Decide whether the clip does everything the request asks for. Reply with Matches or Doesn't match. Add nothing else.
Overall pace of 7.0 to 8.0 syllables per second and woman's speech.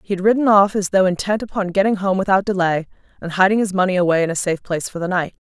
Matches